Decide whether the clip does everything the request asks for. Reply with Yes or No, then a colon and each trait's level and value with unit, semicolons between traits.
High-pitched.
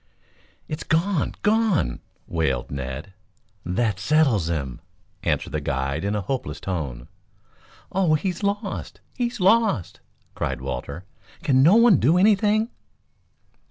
No: medium, 140 Hz